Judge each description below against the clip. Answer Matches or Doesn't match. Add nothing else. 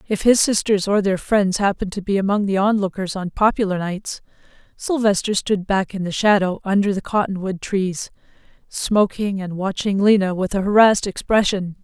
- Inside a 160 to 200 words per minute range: Matches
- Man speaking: Doesn't match